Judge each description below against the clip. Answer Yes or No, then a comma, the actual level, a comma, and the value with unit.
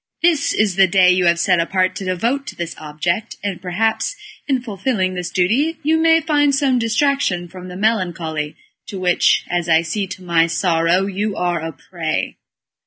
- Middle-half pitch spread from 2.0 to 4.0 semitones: No, average, 4.8 semitones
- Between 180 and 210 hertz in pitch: Yes, medium, 185 Hz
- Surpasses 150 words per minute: Yes, average, 180 wpm